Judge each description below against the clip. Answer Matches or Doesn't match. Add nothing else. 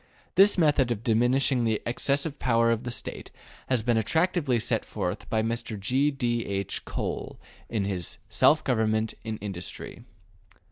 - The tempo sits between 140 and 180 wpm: Matches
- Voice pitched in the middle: Doesn't match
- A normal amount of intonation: Matches